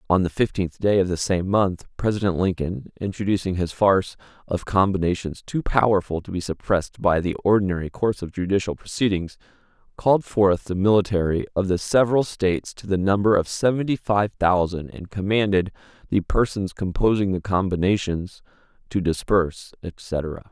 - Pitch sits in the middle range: No, very low, 95 Hz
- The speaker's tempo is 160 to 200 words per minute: No, average, 150 wpm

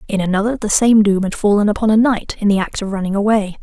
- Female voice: Yes, female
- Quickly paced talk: Yes, fast, 265 wpm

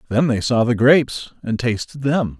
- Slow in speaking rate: No, average, 200 wpm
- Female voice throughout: No, male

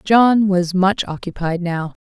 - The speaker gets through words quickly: No, average, 145 wpm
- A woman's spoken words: Yes, female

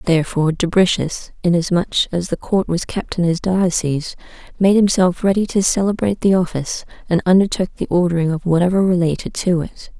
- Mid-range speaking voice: Yes, medium, 180 Hz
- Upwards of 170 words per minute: No, average, 160 wpm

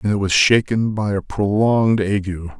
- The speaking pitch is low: Yes, low, 105 Hz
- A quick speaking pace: No, average, 185 wpm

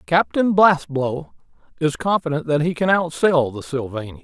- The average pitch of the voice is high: No, medium, 150 Hz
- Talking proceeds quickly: No, average, 140 wpm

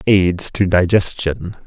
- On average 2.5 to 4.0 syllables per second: Yes, 3.5 syllables/s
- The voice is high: No, very low, 95 Hz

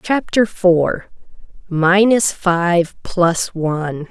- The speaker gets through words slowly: Yes, slow, 75 wpm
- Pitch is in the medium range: Yes, medium, 180 Hz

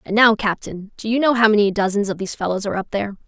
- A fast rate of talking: Yes, fast, 275 wpm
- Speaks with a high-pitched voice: Yes, high, 210 Hz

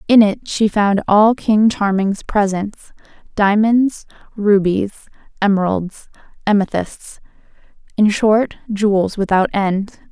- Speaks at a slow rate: Yes, slow, 90 wpm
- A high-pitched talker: Yes, high, 205 Hz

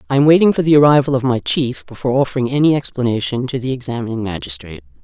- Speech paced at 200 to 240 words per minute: Yes, fast, 205 wpm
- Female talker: Yes, female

